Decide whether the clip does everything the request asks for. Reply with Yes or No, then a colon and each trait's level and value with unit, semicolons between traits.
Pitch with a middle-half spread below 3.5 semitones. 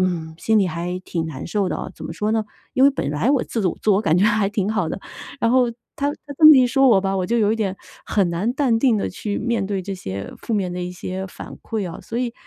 No: average, 4.2 semitones